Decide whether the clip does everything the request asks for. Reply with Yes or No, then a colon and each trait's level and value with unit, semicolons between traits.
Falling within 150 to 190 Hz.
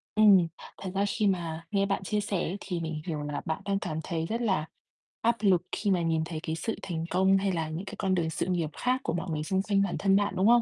Yes: medium, 185 Hz